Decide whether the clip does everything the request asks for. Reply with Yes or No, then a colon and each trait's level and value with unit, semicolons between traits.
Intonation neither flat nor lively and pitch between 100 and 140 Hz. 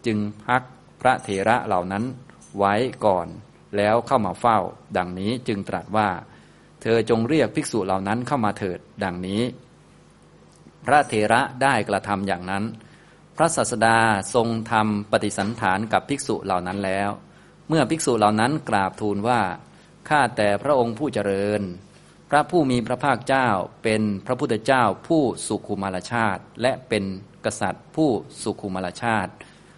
Yes: average, 4.1 semitones; low, 110 Hz